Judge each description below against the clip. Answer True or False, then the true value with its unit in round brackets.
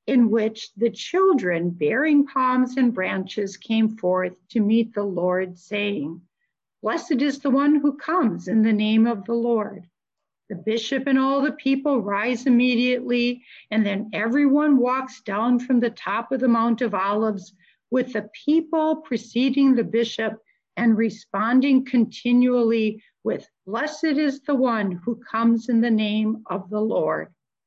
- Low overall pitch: False (230 Hz)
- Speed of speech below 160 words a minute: True (150 wpm)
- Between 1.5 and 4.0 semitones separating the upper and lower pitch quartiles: True (3.6 semitones)